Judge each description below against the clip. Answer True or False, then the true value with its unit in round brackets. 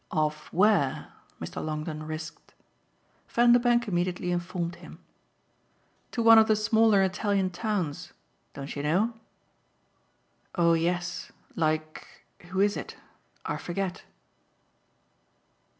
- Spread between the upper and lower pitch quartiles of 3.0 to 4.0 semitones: False (4.7 semitones)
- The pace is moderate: False (105 wpm)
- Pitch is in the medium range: True (180 Hz)